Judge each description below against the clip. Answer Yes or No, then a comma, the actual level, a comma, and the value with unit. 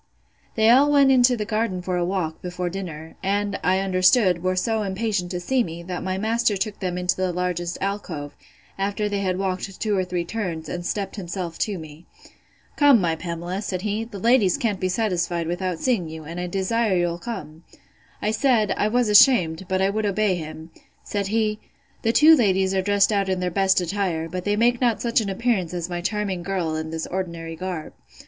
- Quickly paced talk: Yes, fast, 210 wpm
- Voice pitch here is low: No, high, 190 Hz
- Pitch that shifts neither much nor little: Yes, average, 3.2 semitones